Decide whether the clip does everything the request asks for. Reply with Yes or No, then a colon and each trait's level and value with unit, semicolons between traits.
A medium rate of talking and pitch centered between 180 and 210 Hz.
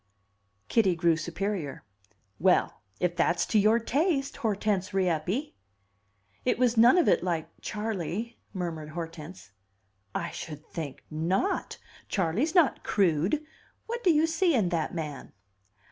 No: slow, 130 wpm; high, 190 Hz